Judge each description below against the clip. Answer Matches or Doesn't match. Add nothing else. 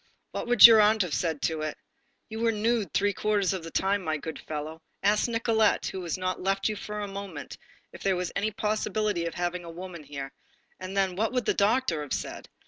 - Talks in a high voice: Matches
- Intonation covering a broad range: Doesn't match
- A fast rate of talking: Matches